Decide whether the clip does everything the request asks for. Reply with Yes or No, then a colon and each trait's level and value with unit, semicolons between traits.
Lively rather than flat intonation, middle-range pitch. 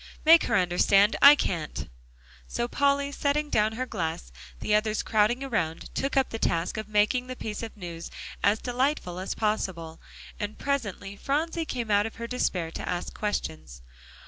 No: wide, 5.7 semitones; high, 215 Hz